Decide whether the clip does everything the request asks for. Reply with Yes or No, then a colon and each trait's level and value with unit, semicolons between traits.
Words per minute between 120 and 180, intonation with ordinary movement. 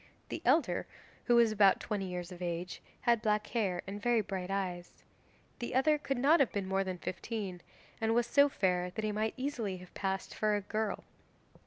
No: average, 195 wpm; average, 4.0 semitones